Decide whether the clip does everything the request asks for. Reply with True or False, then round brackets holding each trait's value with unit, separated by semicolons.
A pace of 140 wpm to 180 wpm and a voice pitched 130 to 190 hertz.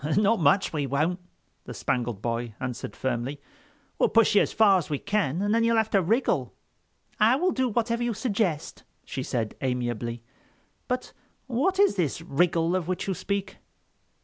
True (175 wpm; 185 Hz)